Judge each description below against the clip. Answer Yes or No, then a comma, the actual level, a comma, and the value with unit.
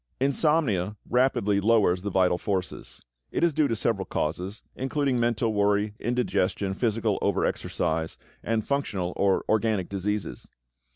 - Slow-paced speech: Yes, slow, 130 wpm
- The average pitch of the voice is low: Yes, low, 105 Hz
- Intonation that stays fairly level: No, average, 4.0 semitones